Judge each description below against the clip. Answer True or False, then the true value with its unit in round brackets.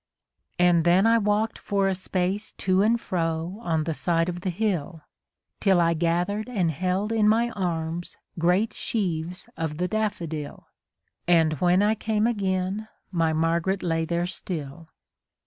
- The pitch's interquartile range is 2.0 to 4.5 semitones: True (3.7 semitones)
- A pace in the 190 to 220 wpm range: False (150 wpm)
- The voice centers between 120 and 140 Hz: False (180 Hz)